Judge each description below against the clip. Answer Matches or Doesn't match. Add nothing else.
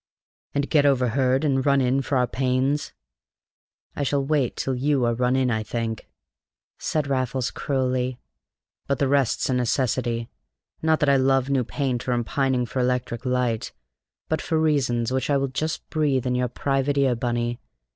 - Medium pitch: Doesn't match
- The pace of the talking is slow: Doesn't match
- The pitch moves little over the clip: Matches